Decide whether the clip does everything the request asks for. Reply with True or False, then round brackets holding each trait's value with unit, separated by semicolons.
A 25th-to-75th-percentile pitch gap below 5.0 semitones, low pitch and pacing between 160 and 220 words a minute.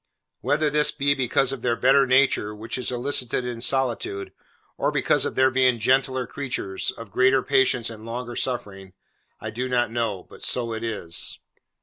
True (2.5 semitones; 125 Hz; 170 wpm)